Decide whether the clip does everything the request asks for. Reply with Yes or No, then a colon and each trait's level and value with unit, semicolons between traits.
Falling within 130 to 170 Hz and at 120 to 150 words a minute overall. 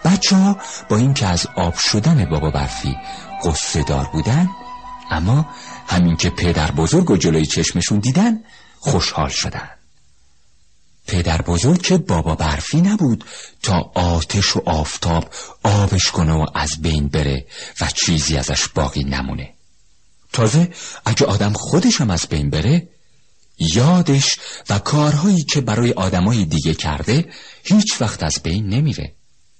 No: very low, 95 Hz; average, 130 wpm